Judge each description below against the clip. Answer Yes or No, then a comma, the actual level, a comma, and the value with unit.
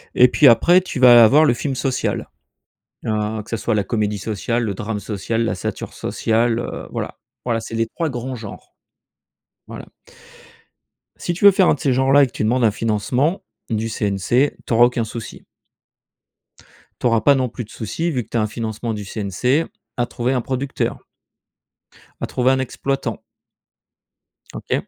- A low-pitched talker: Yes, low, 120 Hz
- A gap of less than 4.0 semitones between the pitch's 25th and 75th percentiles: Yes, average, 3.3 semitones